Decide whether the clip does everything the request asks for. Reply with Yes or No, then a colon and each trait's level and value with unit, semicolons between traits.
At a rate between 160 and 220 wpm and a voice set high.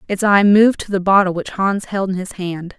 No: fast, 260 wpm; high, 195 Hz